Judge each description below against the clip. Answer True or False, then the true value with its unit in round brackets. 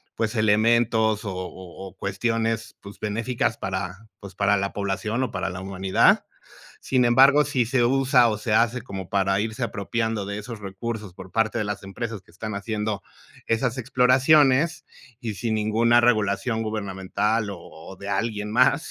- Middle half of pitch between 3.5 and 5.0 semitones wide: False (3.0 semitones)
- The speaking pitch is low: True (110 Hz)